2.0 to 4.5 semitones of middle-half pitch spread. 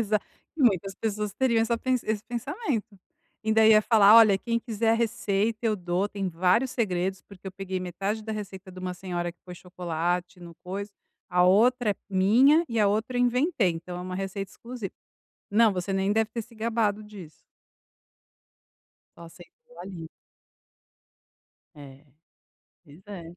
Yes: average, 3.6 semitones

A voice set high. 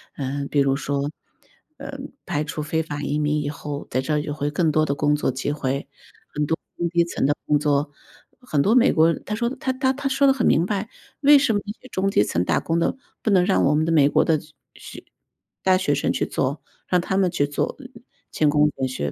No: medium, 150 Hz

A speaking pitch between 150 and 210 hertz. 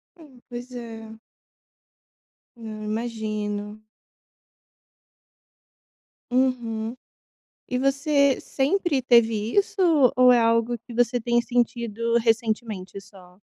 No: high, 235 Hz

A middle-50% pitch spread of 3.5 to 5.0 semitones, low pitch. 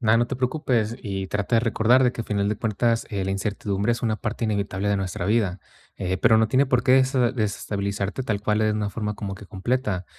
No: average, 2.8 semitones; low, 105 Hz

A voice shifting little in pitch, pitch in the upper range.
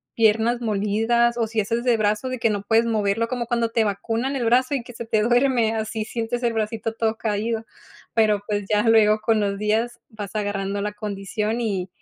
Yes: narrow, 1.9 semitones; high, 225 Hz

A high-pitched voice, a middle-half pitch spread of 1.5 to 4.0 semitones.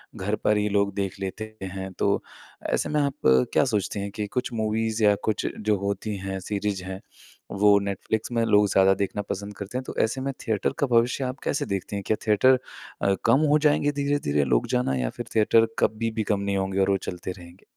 No: low, 105 Hz; average, 2.8 semitones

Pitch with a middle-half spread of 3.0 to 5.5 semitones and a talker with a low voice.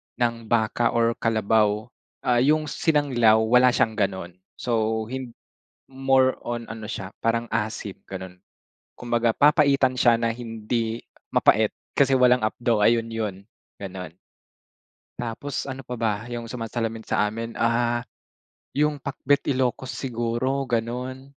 No: narrow, 2.4 semitones; low, 115 Hz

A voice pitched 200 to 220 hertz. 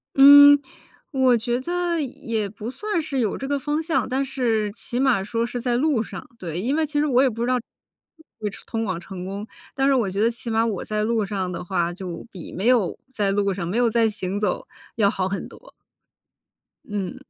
No: high, 230 Hz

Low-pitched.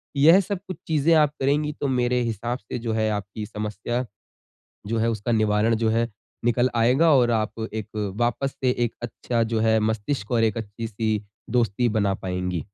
Yes: low, 115 Hz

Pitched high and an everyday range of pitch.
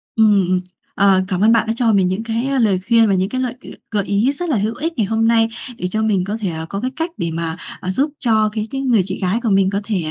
Yes: high, 215 Hz; average, 3.4 semitones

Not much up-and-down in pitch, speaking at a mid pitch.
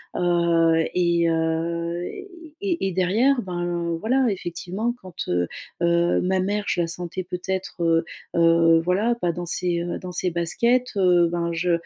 Yes: narrow, 1.7 semitones; medium, 175 Hz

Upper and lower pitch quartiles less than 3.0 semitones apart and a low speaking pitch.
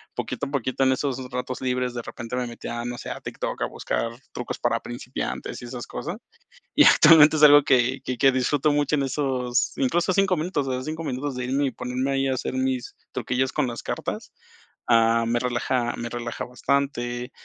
Yes: narrow, 2.4 semitones; low, 130 Hz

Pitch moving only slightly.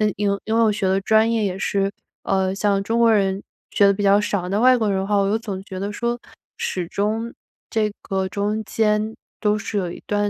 Yes: narrow, 1.9 semitones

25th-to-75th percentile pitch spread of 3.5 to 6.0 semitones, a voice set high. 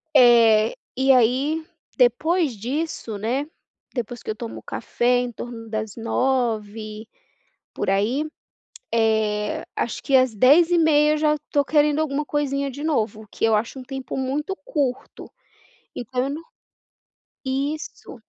Yes: average, 4.6 semitones; very high, 255 Hz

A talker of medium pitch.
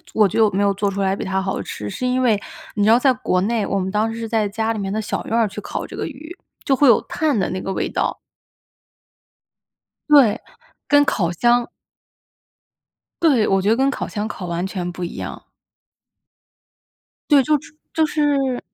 No: high, 220 Hz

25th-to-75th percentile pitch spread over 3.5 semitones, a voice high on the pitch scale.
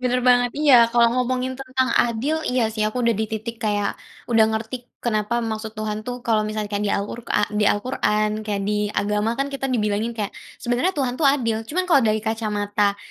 No: average, 3.0 semitones; high, 225 Hz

